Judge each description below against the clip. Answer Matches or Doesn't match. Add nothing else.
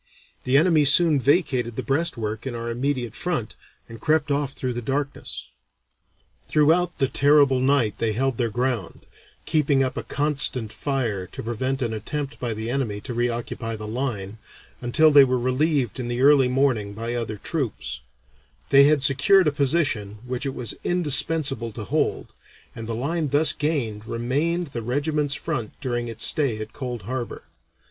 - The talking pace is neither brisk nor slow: Matches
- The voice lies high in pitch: Doesn't match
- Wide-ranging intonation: Doesn't match